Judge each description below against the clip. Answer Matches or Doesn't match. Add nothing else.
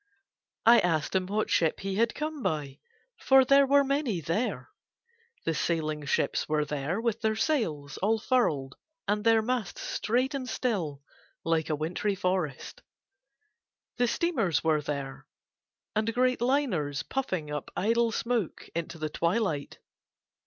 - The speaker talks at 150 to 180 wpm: Doesn't match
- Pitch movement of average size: Doesn't match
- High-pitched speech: Matches